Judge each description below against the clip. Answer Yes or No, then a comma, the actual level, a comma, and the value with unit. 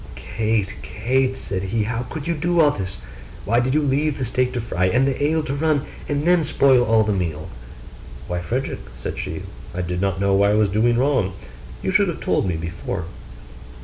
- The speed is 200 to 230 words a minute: Yes, fast, 205 wpm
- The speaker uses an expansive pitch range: Yes, wide, 6.5 semitones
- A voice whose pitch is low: Yes, low, 120 Hz